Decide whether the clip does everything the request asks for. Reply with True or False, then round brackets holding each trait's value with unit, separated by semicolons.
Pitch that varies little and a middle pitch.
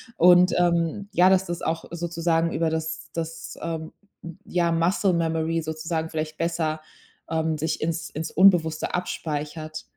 True (1.3 semitones; 165 Hz)